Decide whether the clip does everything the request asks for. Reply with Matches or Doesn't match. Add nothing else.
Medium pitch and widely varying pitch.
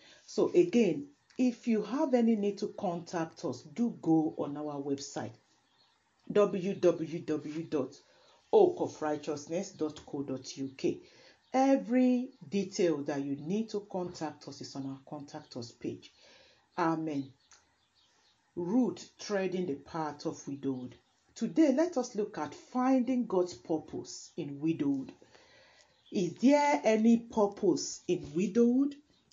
Matches